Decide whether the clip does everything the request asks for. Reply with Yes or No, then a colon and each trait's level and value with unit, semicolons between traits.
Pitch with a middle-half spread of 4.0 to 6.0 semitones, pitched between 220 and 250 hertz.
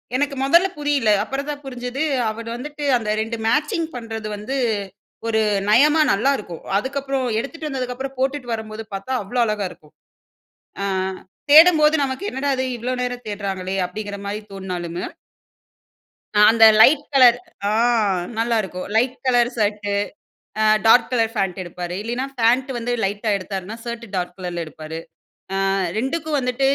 Yes: average, 4.7 semitones; high, 235 Hz